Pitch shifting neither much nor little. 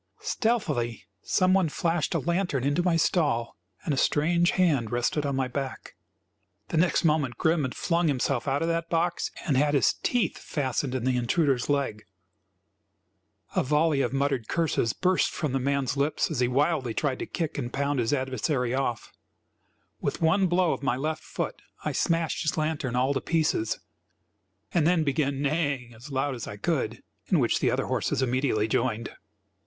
Yes: average, 4.2 semitones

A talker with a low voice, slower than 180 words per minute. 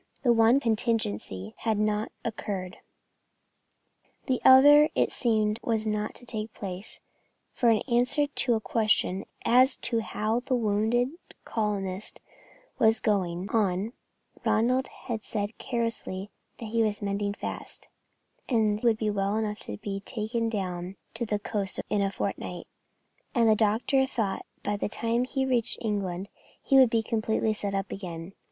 No: high, 215 Hz; average, 150 wpm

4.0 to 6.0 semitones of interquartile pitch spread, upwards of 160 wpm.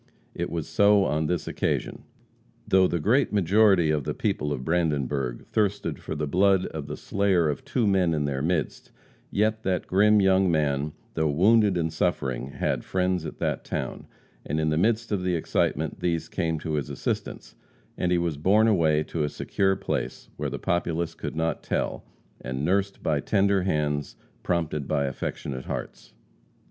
Yes: average, 4.3 semitones; average, 175 wpm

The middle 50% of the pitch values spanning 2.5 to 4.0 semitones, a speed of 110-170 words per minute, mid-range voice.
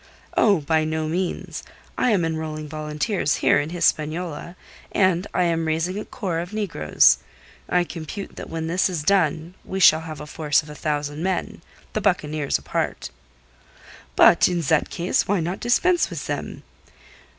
Yes: average, 3.0 semitones; average, 160 wpm; medium, 165 Hz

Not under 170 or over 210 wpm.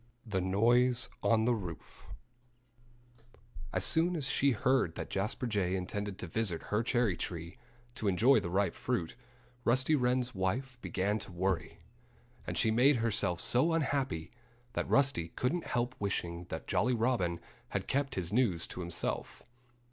No: average, 155 wpm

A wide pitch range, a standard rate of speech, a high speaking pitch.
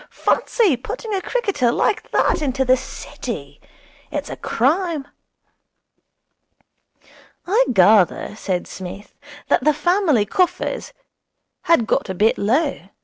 No: wide, 8.9 semitones; slow, 115 wpm; very high, 275 Hz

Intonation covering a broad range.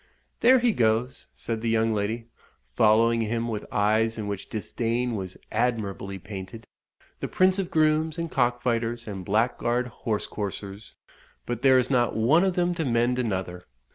No: average, 2.7 semitones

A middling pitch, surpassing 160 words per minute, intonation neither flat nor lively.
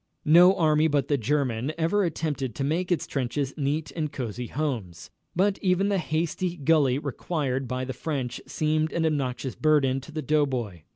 Yes: medium, 150 Hz; average, 170 wpm; average, 3.5 semitones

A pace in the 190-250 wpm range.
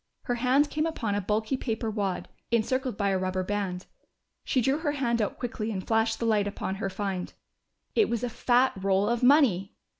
Yes: average, 200 wpm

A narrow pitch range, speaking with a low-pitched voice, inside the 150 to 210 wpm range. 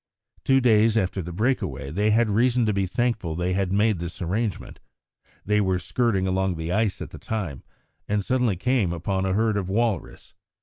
No: average, 3.6 semitones; low, 100 Hz; average, 190 wpm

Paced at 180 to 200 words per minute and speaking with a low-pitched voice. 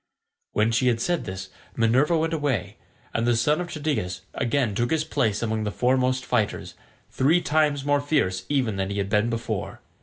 Yes: average, 185 wpm; low, 120 Hz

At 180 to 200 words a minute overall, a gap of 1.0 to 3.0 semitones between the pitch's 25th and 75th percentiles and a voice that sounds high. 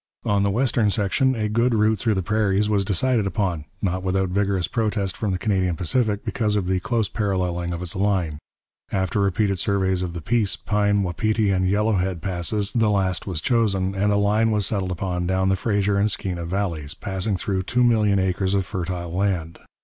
No: average, 195 wpm; narrow, 2.4 semitones; low, 100 Hz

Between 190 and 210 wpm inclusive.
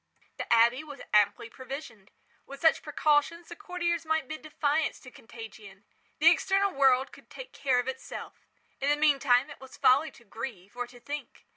No: average, 175 wpm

